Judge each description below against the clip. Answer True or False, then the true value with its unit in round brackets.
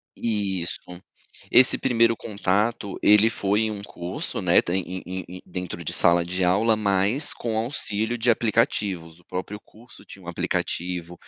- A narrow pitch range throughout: False (3.6 semitones)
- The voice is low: True (100 Hz)